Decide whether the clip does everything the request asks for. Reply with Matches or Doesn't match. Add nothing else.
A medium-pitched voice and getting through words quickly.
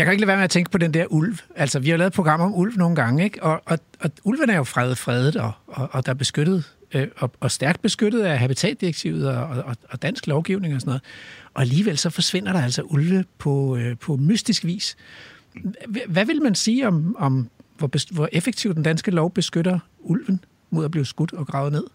Matches